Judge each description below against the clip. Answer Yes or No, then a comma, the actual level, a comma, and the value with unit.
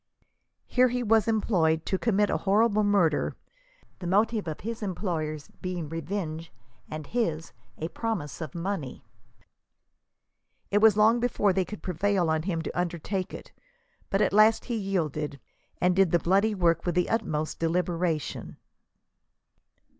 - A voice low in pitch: No, medium, 185 Hz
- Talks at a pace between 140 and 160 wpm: Yes, average, 145 wpm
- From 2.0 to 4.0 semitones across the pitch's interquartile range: No, average, 4.4 semitones